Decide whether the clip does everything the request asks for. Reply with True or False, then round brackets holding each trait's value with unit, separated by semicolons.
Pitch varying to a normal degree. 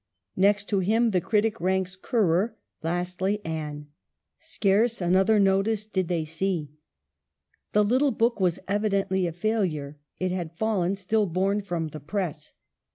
True (3.4 semitones)